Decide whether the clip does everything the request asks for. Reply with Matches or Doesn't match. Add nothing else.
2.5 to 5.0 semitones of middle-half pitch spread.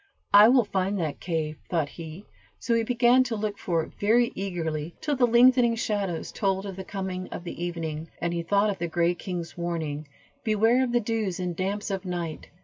Matches